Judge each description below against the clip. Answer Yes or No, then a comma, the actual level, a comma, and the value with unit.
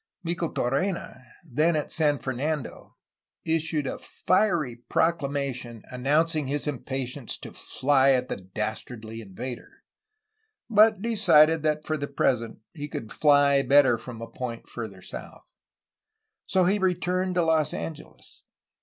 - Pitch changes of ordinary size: Yes, average, 4.6 semitones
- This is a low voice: No, medium, 145 Hz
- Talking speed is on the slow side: Yes, slow, 130 wpm